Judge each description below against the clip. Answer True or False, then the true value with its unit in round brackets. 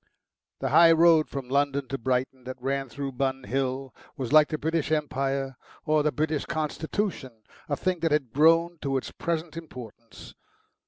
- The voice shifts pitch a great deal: False (3.1 semitones)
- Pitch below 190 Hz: True (140 Hz)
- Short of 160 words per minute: False (165 wpm)